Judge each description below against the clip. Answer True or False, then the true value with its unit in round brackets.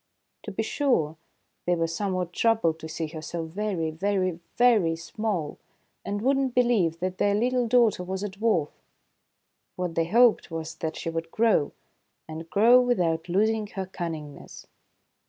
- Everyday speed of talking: True (155 wpm)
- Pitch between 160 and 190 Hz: True (185 Hz)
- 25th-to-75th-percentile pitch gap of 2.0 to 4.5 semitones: False (5.2 semitones)